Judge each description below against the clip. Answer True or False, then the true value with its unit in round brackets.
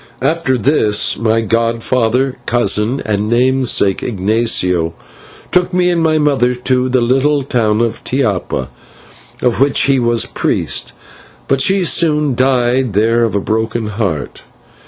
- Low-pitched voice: True (120 Hz)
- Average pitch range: True (3.5 semitones)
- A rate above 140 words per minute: False (135 wpm)